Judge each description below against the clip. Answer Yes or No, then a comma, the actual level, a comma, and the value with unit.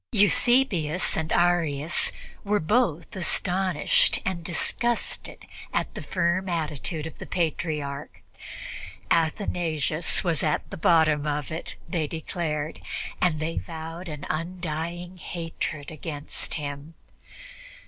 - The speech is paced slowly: Yes, slow, 105 wpm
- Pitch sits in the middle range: Yes, medium, 165 Hz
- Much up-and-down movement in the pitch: No, narrow, 2.5 semitones